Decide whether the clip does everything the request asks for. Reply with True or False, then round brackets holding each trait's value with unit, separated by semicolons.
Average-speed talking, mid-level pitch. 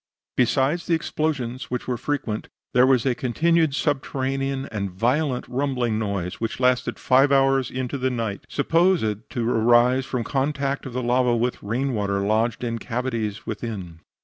False (155 wpm; 125 Hz)